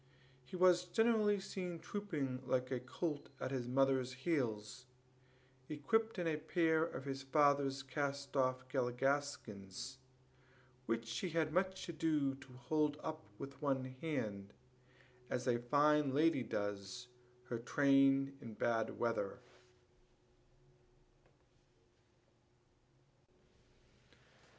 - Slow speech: Yes, slow, 105 wpm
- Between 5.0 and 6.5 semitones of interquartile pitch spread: No, average, 3.8 semitones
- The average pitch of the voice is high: No, low, 135 Hz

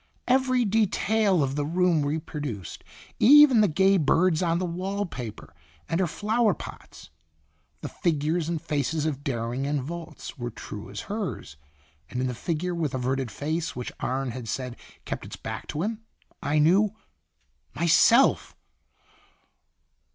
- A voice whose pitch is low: No, medium, 160 Hz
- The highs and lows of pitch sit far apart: Yes, wide, 5.9 semitones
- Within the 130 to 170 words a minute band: Yes, average, 150 wpm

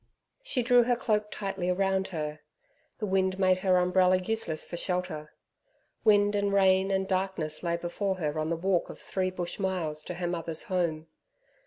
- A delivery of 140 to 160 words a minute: No, average, 175 wpm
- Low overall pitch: No, medium, 185 Hz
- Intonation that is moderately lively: No, narrow, 2.1 semitones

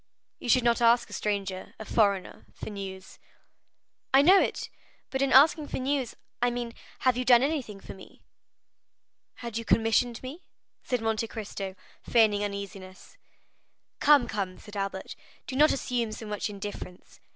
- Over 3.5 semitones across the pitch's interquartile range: Yes, average, 4.1 semitones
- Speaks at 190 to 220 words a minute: No, average, 155 wpm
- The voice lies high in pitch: Yes, high, 225 Hz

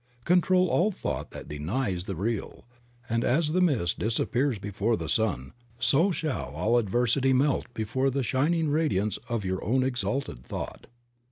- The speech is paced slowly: No, average, 155 wpm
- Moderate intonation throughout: No, wide, 6.0 semitones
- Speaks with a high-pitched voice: No, low, 120 Hz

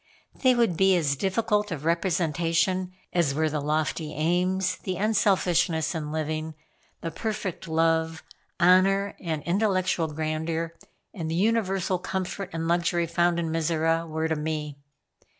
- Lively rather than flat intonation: No, average, 2.7 semitones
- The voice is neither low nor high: Yes, medium, 170 Hz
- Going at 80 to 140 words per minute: Yes, slow, 135 wpm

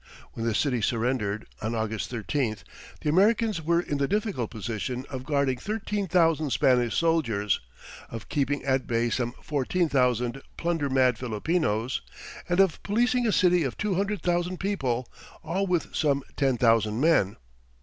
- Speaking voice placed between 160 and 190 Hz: No, medium, 140 Hz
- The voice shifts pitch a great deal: Yes, wide, 6.7 semitones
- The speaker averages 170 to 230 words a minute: No, average, 155 wpm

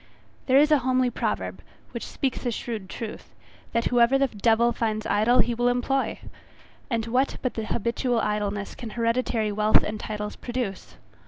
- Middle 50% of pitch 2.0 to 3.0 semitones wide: Yes, narrow, 2.6 semitones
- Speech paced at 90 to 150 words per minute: No, average, 160 wpm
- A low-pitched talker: No, high, 235 Hz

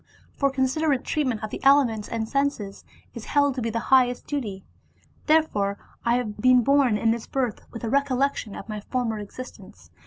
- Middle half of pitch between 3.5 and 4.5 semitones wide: Yes, average, 3.9 semitones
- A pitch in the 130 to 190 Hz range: No, very high, 250 Hz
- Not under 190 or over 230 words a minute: No, average, 180 wpm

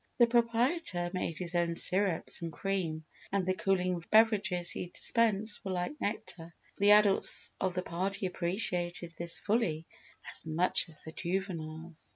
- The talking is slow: No, average, 150 wpm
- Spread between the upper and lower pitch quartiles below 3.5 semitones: Yes, average, 3.0 semitones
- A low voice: No, medium, 185 Hz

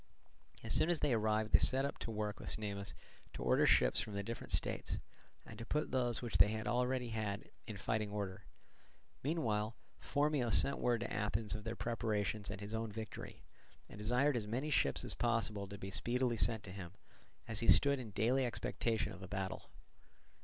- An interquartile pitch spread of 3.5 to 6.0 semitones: No, average, 2.9 semitones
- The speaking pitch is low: Yes, low, 110 Hz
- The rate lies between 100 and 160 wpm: No, average, 190 wpm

